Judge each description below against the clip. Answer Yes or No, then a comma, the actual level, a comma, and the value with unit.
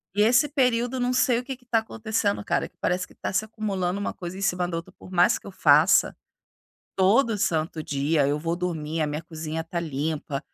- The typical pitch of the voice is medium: Yes, medium, 180 Hz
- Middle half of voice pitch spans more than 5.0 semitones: Yes, wide, 5.4 semitones